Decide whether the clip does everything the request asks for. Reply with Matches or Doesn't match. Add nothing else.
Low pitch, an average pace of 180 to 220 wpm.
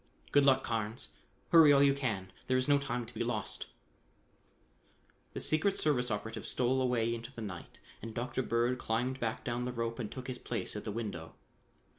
Matches